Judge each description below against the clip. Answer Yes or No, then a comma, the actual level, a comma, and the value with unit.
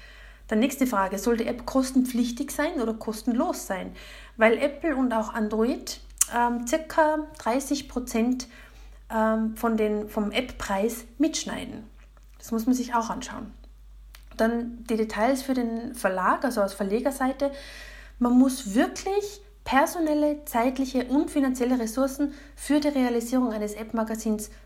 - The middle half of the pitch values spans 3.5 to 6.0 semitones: Yes, average, 3.9 semitones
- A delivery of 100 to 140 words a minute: Yes, average, 130 wpm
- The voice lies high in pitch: Yes, high, 245 Hz